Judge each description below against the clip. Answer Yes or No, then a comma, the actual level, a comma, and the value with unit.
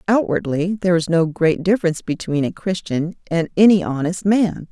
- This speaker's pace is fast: No, average, 165 wpm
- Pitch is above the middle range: No, medium, 175 Hz